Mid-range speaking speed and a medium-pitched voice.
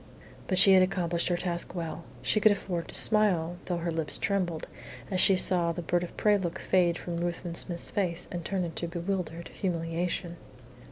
Yes: average, 185 wpm; medium, 175 Hz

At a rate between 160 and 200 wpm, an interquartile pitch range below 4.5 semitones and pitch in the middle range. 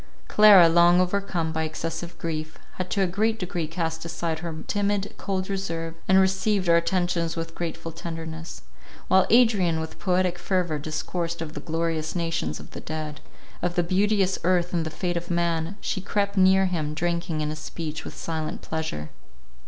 Yes: average, 175 wpm; narrow, 2.6 semitones; medium, 170 Hz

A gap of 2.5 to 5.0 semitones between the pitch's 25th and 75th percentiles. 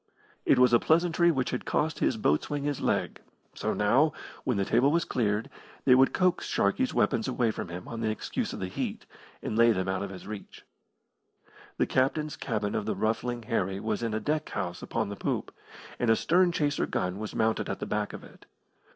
No: wide, 5.6 semitones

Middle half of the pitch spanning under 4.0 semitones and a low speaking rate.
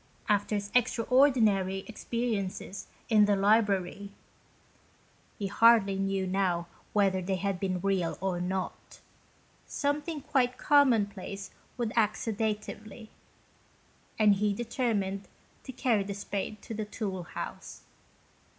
Yes: average, 2.8 semitones; slow, 115 wpm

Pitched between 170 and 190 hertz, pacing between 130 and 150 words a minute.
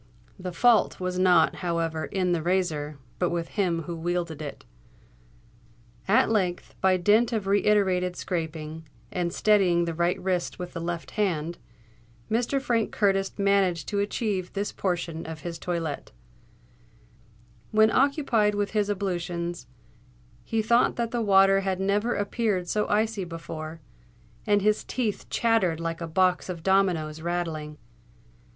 Yes: medium, 185 Hz; average, 145 wpm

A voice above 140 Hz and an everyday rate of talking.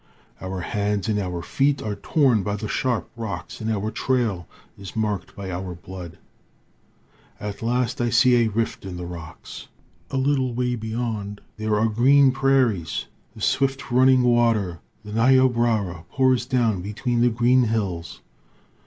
No: low, 110 Hz; average, 155 wpm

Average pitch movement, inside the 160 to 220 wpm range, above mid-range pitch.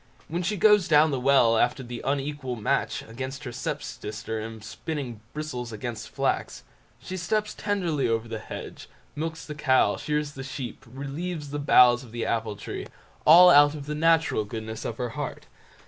No: average, 4.8 semitones; average, 175 wpm; low, 135 Hz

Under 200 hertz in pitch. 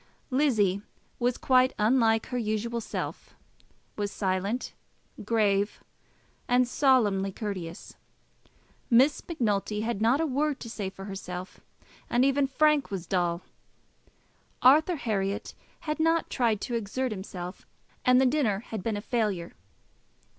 No: high, 225 Hz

